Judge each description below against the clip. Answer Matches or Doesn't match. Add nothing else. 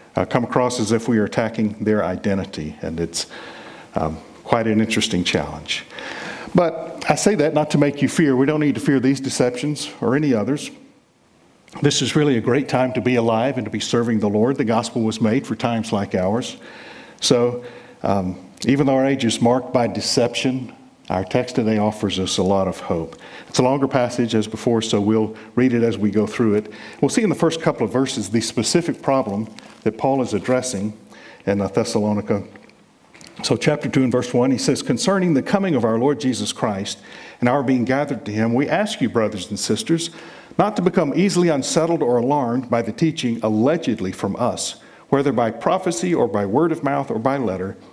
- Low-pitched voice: Matches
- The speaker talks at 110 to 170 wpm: Doesn't match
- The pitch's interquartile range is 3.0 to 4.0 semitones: Doesn't match